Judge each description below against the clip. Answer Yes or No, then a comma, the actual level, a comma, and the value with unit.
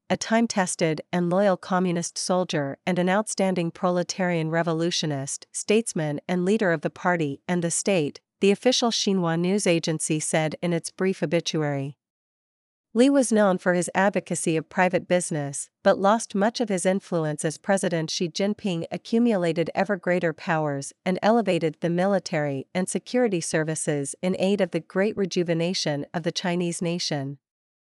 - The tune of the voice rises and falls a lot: No, average, 2.9 semitones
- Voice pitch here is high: No, medium, 180 Hz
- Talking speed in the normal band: No, slow, 155 wpm